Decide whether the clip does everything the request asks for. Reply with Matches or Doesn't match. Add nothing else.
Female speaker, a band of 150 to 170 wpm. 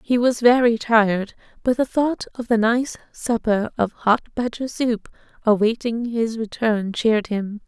Matches